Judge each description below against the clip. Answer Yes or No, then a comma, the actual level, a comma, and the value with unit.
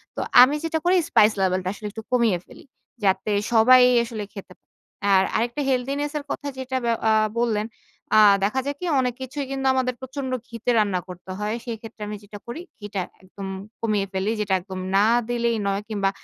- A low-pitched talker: No, high, 225 Hz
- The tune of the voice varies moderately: Yes, average, 4.0 semitones